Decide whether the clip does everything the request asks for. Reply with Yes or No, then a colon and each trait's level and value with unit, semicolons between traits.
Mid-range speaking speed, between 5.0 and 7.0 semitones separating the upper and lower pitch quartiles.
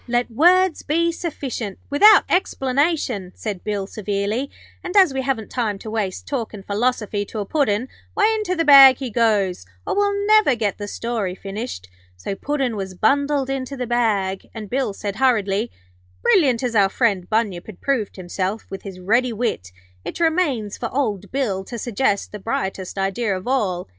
Yes: average, 175 wpm; wide, 5.4 semitones